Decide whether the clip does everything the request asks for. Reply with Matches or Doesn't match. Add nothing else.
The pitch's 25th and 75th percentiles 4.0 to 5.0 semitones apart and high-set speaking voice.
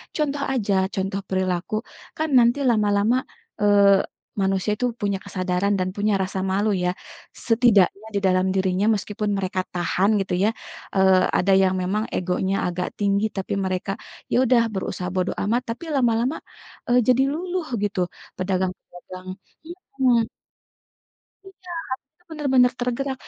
Matches